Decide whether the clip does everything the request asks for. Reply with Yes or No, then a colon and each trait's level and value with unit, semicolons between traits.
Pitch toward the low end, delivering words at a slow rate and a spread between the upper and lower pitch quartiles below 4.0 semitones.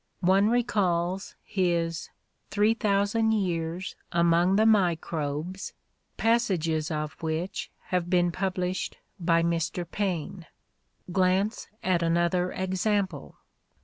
No: medium, 180 Hz; slow, 95 wpm; average, 2.8 semitones